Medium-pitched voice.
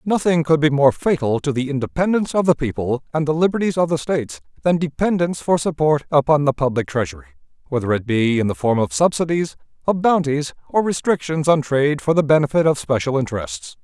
Yes: medium, 145 Hz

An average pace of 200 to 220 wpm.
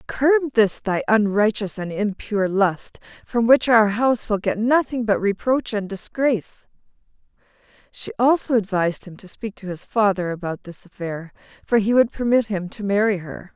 No: average, 170 wpm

